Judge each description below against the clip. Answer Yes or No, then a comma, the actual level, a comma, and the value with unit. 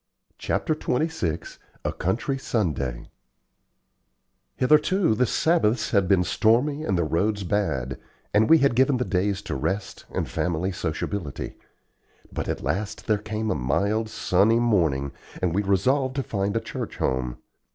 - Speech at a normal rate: Yes, average, 145 wpm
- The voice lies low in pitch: Yes, low, 100 Hz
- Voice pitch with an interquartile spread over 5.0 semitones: Yes, wide, 5.4 semitones